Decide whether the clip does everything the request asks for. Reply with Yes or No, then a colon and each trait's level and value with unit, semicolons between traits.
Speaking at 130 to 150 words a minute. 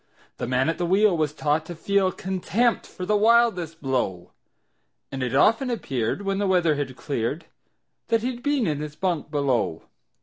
No: average, 175 wpm